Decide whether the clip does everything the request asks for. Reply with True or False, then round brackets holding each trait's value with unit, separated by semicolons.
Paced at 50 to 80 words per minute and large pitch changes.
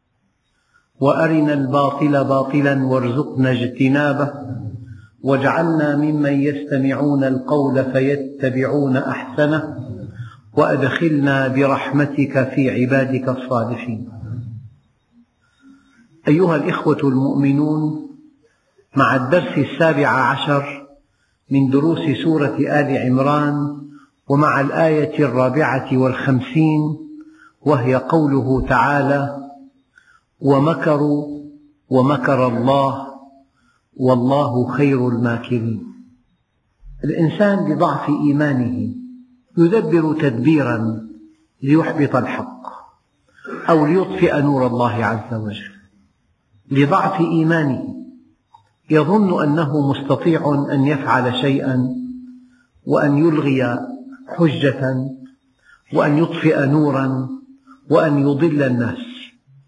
False (70 wpm; 2.8 semitones)